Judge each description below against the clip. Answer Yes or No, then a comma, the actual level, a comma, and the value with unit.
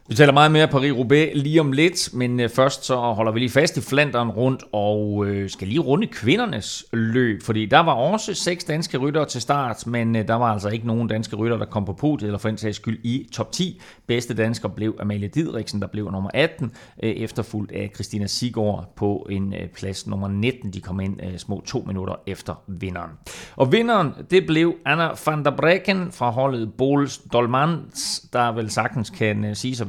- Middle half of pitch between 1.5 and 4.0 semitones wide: No, average, 5.3 semitones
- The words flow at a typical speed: Yes, average, 195 wpm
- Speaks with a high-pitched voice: No, low, 120 Hz